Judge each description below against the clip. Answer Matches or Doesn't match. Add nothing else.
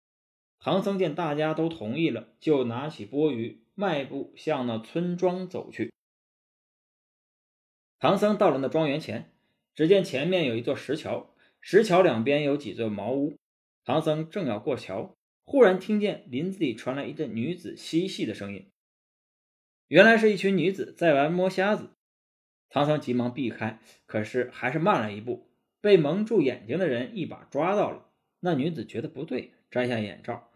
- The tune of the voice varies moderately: Doesn't match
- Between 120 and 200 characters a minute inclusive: Doesn't match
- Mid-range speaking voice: Matches